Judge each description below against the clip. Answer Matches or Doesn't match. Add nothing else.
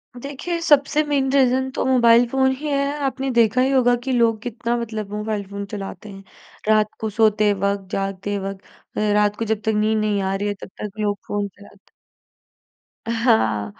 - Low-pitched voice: Doesn't match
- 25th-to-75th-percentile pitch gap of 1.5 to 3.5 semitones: Doesn't match